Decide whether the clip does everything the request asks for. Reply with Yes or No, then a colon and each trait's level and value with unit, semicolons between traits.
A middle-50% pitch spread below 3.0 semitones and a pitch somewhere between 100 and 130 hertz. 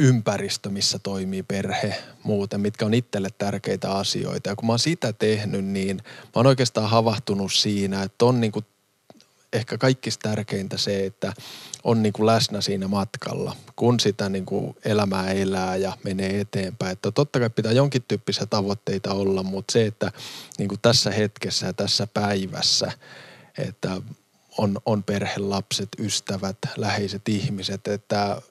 Yes: narrow, 2.6 semitones; low, 105 Hz